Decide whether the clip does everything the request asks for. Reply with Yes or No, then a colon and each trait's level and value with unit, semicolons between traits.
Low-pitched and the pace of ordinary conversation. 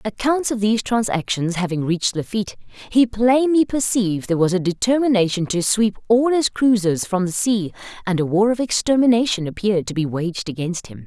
No: high, 205 Hz; average, 180 wpm